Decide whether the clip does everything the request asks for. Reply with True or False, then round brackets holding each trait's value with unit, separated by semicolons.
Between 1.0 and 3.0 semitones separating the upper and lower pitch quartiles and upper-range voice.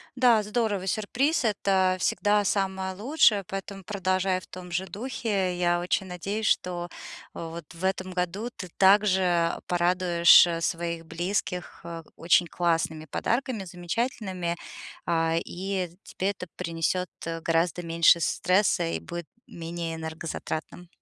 False (2.6 semitones; 180 Hz)